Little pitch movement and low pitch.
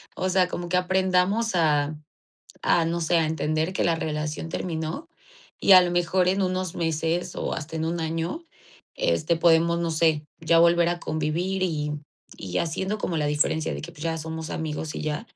No: narrow, 2.3 semitones; medium, 165 Hz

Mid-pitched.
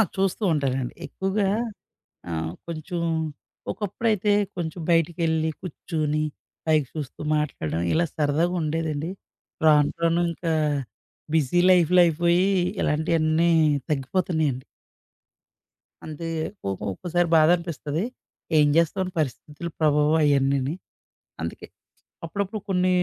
Yes: medium, 160 Hz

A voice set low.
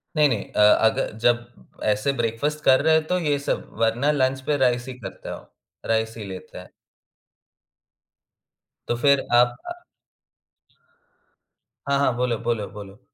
Yes: low, 120 Hz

